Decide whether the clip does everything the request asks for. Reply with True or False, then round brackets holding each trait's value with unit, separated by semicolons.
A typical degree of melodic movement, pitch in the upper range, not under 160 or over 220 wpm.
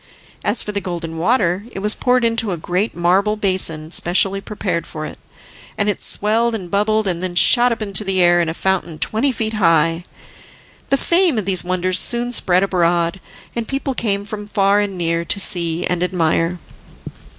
True (3.7 semitones; 195 Hz; 185 wpm)